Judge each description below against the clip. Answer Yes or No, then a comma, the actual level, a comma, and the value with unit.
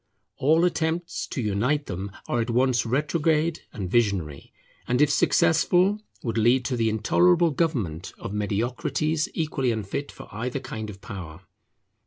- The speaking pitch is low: Yes, low, 125 Hz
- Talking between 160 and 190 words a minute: No, average, 145 wpm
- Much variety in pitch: Yes, wide, 6.5 semitones